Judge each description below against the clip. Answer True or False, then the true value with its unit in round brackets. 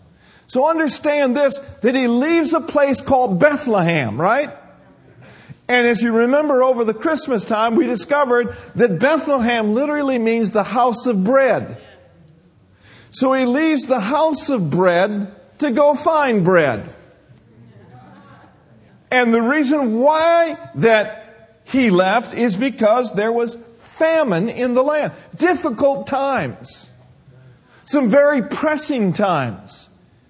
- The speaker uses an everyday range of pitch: True (4.8 semitones)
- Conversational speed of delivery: False (120 wpm)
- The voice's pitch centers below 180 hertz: False (255 Hz)